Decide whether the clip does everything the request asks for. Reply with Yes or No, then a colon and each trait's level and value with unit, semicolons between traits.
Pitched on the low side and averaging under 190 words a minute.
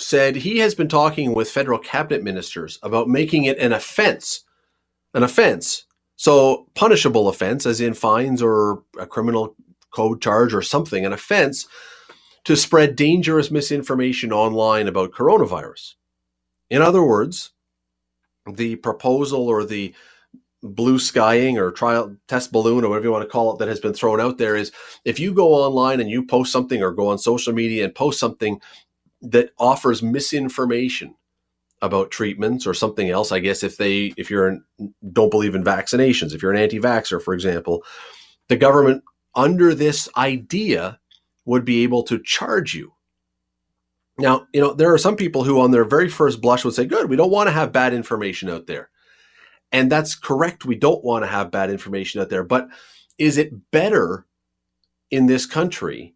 Yes: low, 120 Hz; average, 170 wpm